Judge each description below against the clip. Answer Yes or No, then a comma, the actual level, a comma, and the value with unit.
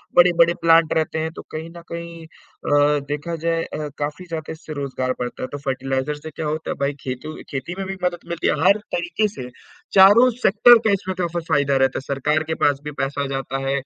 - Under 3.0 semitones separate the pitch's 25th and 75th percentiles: No, average, 3.4 semitones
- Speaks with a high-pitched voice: No, medium, 155 Hz